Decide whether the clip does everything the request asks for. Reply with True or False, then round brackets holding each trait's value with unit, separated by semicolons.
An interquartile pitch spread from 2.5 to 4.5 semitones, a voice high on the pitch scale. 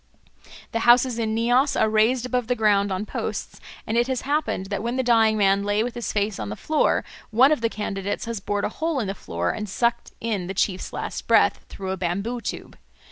True (3.3 semitones; 220 Hz)